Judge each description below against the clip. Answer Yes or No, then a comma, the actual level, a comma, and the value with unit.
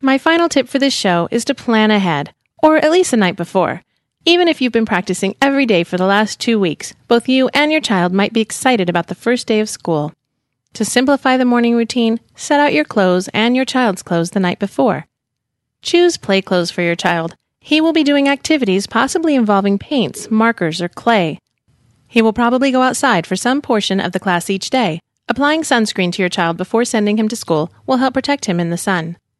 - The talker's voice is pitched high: Yes, high, 220 Hz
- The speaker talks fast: Yes, fast, 215 wpm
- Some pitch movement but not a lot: No, wide, 6.5 semitones